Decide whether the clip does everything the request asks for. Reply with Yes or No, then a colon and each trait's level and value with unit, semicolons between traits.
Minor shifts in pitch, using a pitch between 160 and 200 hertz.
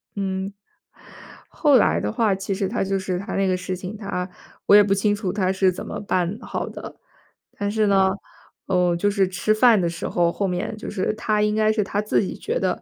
Yes: narrow, 2.2 semitones; high, 195 Hz